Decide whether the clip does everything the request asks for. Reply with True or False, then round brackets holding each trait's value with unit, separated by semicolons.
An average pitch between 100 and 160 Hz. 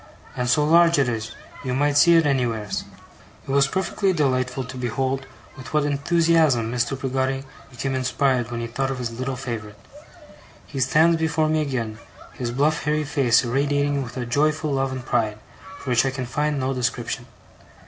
True (135 Hz)